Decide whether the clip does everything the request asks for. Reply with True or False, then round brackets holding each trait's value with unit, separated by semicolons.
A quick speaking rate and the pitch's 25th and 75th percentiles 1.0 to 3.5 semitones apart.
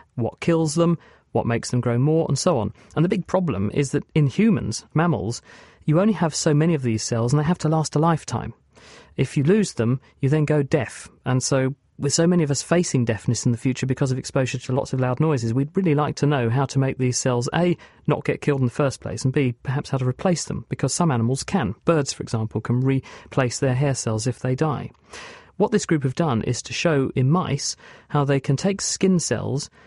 False (240 wpm; 4.2 semitones)